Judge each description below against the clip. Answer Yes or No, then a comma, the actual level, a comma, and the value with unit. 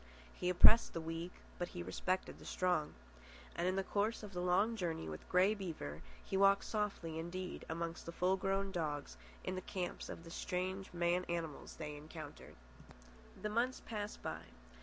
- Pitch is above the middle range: No, medium, 180 Hz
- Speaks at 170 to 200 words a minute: Yes, average, 175 wpm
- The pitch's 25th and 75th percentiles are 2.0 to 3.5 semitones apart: Yes, average, 2.8 semitones